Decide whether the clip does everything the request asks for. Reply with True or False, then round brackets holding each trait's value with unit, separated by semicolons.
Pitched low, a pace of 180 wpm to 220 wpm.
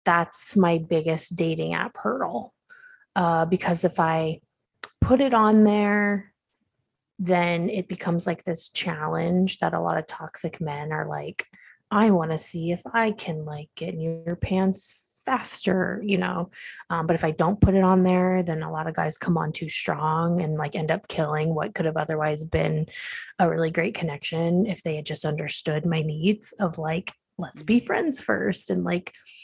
False (170 Hz; 185 wpm)